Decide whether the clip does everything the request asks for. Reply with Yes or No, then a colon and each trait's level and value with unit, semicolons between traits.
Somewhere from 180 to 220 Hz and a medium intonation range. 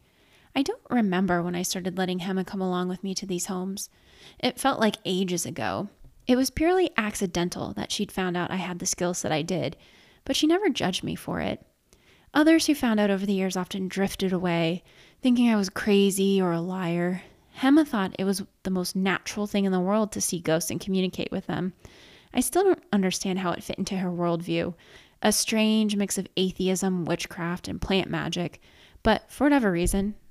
Yes: high, 190 Hz; average, 3.0 semitones